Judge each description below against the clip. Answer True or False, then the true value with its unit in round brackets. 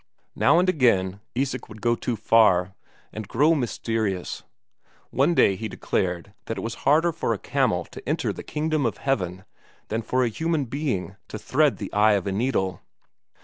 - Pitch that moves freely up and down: True (5.9 semitones)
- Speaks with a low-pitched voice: True (115 Hz)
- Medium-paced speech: True (180 wpm)